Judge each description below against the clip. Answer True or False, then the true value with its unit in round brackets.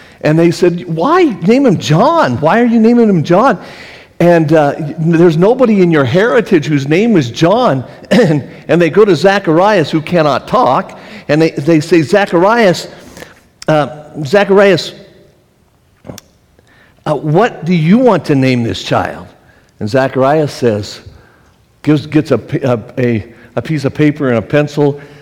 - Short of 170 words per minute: True (150 wpm)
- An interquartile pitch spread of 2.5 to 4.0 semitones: False (4.5 semitones)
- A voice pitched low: False (155 Hz)